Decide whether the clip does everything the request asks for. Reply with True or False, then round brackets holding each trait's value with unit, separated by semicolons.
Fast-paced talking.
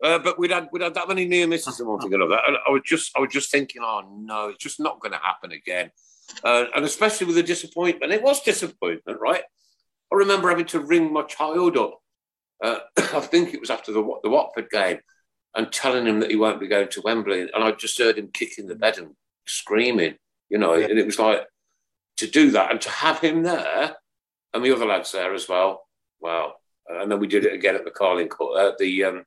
True (230 wpm)